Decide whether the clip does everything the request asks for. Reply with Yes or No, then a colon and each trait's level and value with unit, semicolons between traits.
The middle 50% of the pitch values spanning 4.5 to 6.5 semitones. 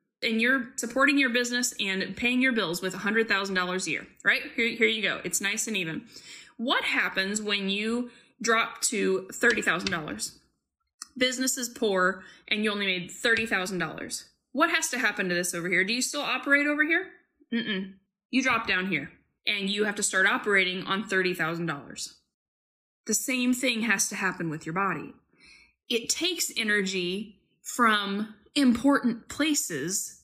Yes: average, 5.0 semitones